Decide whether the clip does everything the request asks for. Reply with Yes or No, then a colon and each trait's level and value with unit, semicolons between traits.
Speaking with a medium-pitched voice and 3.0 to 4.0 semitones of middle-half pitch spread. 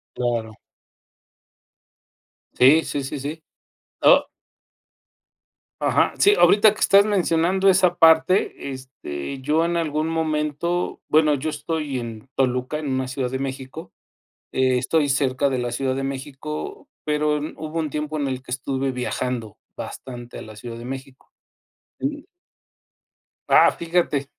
Yes: medium, 145 Hz; average, 3.7 semitones